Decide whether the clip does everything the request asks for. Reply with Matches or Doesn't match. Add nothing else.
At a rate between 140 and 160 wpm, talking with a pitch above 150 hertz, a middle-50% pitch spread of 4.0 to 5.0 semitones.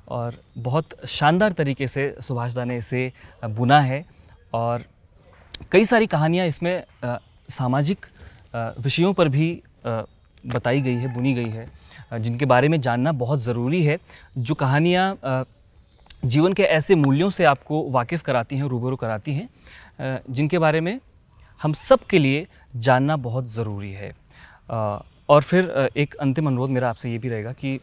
Doesn't match